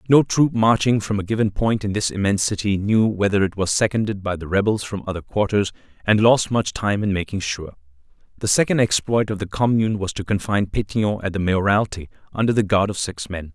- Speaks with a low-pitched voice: Yes, low, 105 Hz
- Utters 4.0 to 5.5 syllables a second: No, 5.8 syllables/s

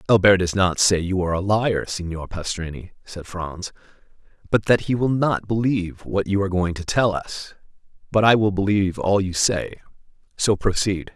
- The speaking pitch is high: No, very low, 95 Hz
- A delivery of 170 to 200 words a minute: Yes, average, 180 wpm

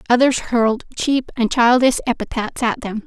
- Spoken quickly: No, average, 155 wpm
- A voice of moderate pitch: No, high, 240 Hz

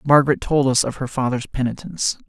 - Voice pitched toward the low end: Yes, low, 130 Hz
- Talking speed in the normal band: Yes, average, 185 wpm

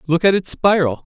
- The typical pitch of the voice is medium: Yes, medium, 175 Hz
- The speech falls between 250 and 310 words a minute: No, fast, 220 wpm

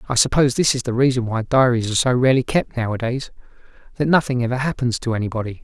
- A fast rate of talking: No, average, 190 wpm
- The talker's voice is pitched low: Yes, low, 125 Hz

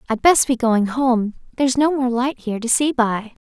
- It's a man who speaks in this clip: No, female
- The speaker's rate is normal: No, fast, 225 wpm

